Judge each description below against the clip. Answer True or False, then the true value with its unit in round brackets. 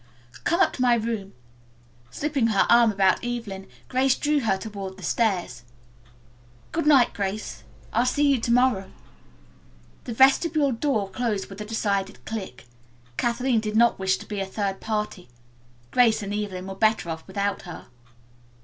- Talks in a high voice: True (220 Hz)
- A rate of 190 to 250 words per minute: False (160 wpm)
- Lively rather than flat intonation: False (4.1 semitones)